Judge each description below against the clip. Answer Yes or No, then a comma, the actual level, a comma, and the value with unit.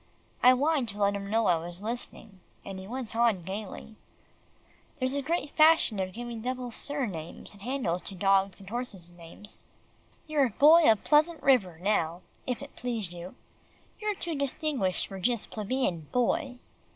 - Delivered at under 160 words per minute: No, average, 165 wpm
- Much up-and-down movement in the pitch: Yes, wide, 5.7 semitones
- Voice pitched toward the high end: Yes, high, 225 Hz